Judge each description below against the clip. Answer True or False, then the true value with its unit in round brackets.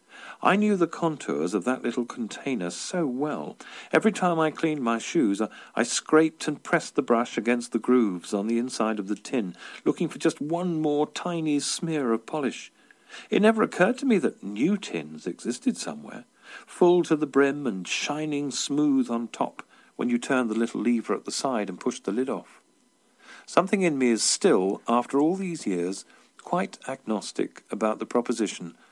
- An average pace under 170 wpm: False (185 wpm)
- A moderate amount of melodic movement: False (5.8 semitones)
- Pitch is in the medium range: False (130 Hz)